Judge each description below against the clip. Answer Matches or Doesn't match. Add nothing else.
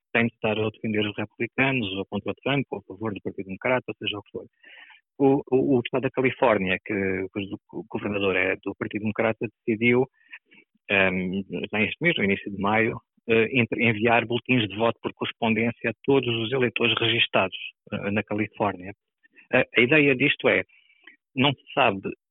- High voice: Doesn't match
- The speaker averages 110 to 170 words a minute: Doesn't match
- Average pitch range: Matches